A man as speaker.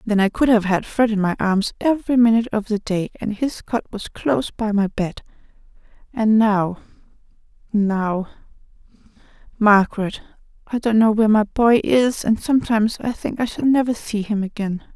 No: female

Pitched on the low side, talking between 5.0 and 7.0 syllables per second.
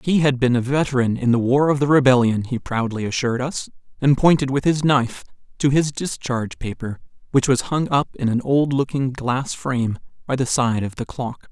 Yes: low, 130 Hz; 5.3 syllables/s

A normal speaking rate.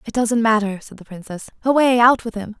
No: fast, 230 wpm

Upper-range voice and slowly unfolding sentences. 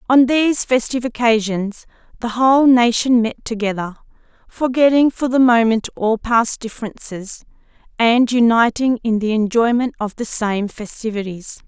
Yes: high, 230 Hz; slow, 130 wpm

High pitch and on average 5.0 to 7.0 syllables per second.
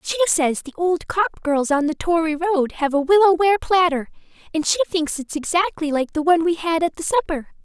Yes: very high, 330 Hz; 5.5 syllables/s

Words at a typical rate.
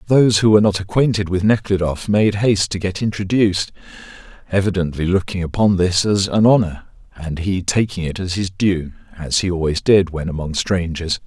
Yes: average, 175 wpm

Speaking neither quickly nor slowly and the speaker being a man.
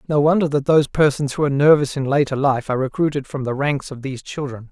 No: fast, 240 wpm; male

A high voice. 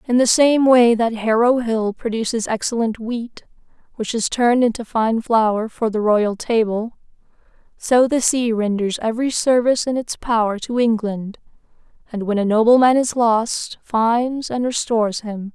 Yes: high, 230 Hz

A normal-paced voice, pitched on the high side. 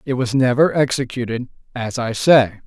No: average, 160 wpm; low, 125 Hz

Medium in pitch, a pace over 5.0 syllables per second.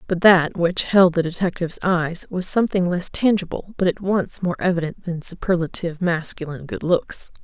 Yes: medium, 175 Hz; 5.2 syllables/s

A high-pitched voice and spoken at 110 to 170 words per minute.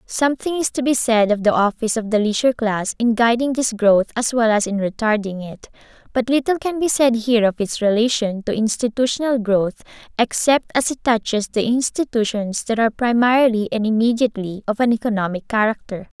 No: high, 230 Hz; average, 180 wpm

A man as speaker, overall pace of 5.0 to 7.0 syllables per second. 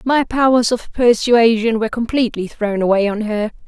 No: female; 5.2 syllables/s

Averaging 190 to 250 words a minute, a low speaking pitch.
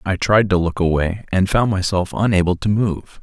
Yes: fast, 205 wpm; very low, 95 Hz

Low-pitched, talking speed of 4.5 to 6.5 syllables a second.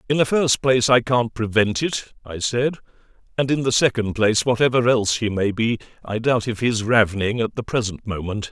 Yes: low, 115 Hz; 5.5 syllables/s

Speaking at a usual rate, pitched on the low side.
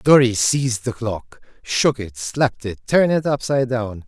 Yes: average, 145 wpm; low, 120 Hz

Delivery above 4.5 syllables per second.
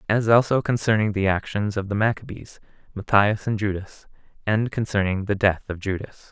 Yes: 5.2 syllables/s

